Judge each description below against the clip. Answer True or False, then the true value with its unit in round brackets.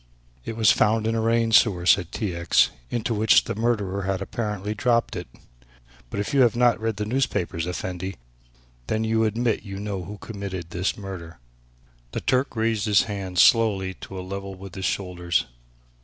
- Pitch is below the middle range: True (105 Hz)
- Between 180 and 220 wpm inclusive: True (185 wpm)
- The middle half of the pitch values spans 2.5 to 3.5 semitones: True (3.1 semitones)